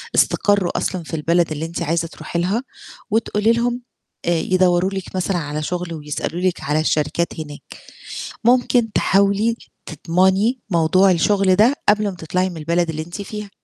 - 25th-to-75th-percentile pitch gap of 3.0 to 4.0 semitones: Yes, average, 3.6 semitones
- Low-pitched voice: No, medium, 180 Hz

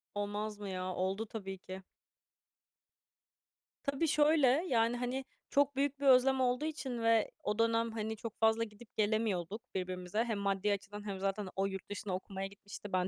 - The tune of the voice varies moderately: Yes, average, 3.9 semitones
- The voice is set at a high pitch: Yes, high, 215 Hz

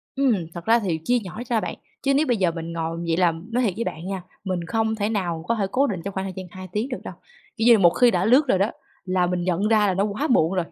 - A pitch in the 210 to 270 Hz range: No, high, 195 Hz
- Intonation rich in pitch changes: No, average, 4.4 semitones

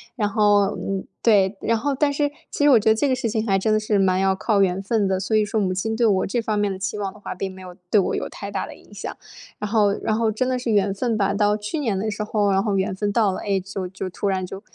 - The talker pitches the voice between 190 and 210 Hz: Yes, high, 205 Hz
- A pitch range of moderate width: No, narrow, 2.3 semitones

